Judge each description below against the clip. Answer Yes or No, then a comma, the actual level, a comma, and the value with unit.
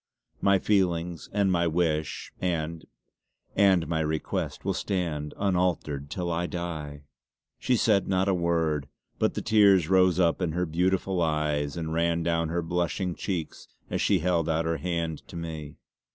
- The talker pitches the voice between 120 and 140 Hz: No, very low, 85 Hz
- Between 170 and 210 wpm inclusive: No, average, 160 wpm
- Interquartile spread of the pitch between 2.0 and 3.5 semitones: Yes, narrow, 2.4 semitones